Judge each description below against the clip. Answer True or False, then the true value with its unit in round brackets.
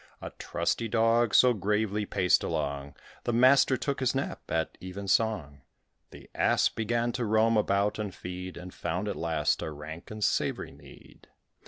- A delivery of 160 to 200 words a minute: True (165 wpm)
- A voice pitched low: True (105 Hz)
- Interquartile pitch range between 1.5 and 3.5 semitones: False (4.4 semitones)